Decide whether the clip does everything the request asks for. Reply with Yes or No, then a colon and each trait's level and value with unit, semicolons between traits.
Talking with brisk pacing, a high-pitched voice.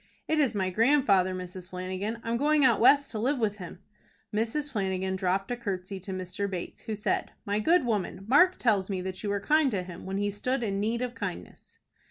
Yes: fast, 215 wpm; high, 205 Hz